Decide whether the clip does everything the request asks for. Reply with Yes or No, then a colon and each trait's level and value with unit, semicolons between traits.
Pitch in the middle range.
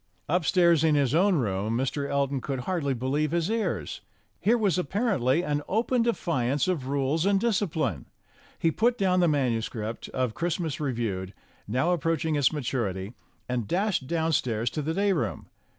Yes: medium, 150 Hz